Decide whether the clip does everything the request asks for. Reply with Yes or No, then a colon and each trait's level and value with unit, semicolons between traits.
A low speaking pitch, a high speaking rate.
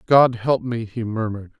No: low, 115 Hz; average, 190 wpm